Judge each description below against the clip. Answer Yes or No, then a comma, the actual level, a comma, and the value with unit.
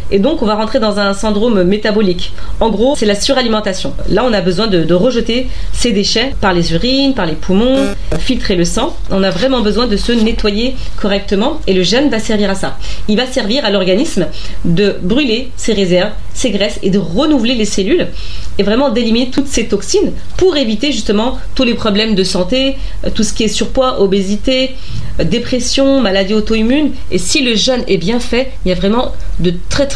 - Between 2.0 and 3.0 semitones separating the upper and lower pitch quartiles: No, average, 4.4 semitones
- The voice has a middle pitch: No, high, 220 Hz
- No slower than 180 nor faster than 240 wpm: Yes, average, 200 wpm